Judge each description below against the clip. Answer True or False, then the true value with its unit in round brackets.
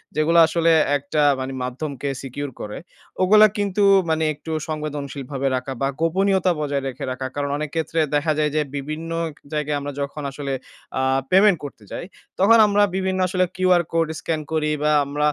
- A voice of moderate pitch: True (150 Hz)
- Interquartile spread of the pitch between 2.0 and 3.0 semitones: False (3.4 semitones)